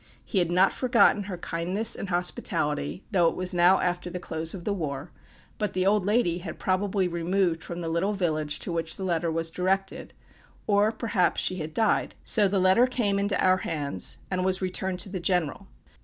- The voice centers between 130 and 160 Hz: No, medium, 185 Hz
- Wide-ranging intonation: No, average, 2.7 semitones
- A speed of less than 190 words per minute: No, average, 200 wpm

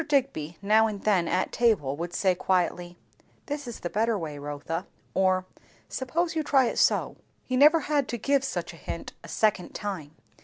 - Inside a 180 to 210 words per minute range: Yes, average, 185 wpm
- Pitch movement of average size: No, wide, 7.0 semitones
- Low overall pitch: No, high, 205 Hz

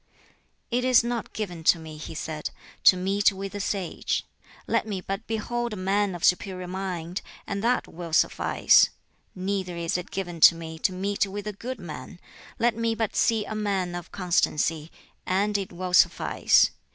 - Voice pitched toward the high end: Yes, high, 195 Hz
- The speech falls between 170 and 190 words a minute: Yes, average, 175 wpm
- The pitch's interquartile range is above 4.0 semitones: No, average, 3.0 semitones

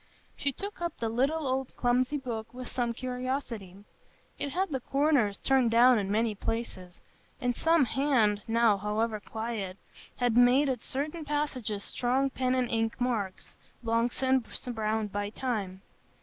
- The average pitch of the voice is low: No, high, 245 Hz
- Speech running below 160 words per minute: Yes, average, 150 wpm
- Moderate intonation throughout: Yes, average, 3.4 semitones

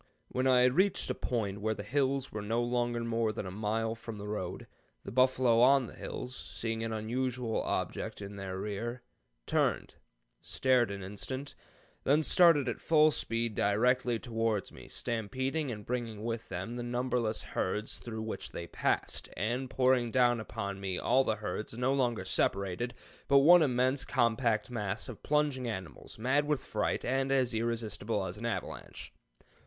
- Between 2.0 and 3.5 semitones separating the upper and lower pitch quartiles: Yes, average, 3.2 semitones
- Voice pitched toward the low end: Yes, low, 115 Hz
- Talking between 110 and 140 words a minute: No, average, 170 wpm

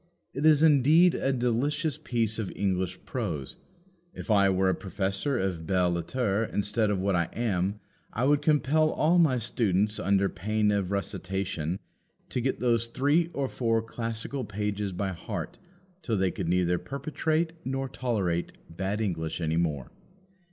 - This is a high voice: No, low, 105 Hz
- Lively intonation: Yes, wide, 5.7 semitones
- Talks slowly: No, average, 155 wpm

